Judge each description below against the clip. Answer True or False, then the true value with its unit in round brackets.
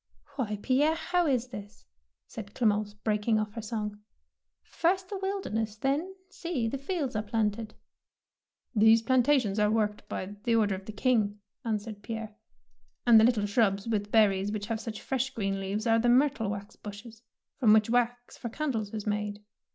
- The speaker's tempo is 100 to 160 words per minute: False (180 wpm)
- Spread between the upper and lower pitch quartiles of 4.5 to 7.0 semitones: False (3.3 semitones)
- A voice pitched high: True (220 Hz)